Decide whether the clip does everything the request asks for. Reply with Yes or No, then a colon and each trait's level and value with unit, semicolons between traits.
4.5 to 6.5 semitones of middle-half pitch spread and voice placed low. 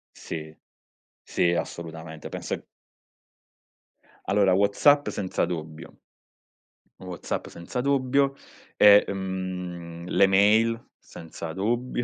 Yes: average, 4.9 semitones; very low, 95 Hz